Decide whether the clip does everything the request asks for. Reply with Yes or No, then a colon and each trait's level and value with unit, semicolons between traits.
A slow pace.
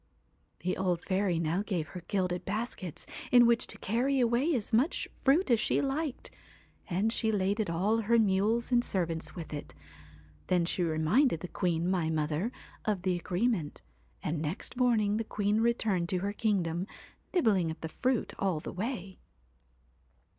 No: average, 160 wpm